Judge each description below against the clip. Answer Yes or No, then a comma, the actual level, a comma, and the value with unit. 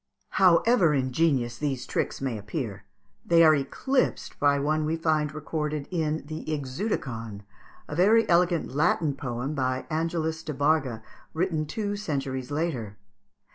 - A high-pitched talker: No, medium, 150 Hz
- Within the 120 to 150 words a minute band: Yes, slow, 135 wpm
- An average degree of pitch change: Yes, average, 3.8 semitones